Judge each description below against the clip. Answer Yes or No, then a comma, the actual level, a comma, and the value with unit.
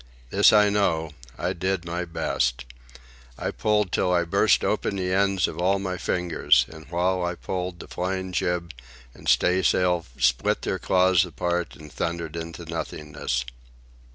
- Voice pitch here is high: No, very low, 90 Hz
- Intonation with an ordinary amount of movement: No, narrow, 2.1 semitones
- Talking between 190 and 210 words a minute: No, average, 155 wpm